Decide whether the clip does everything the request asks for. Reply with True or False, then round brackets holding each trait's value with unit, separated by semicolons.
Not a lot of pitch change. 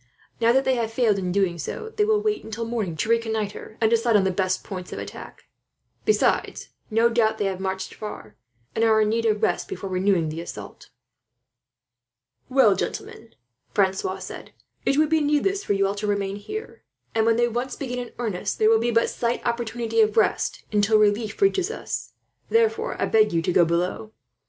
False (3.4 semitones)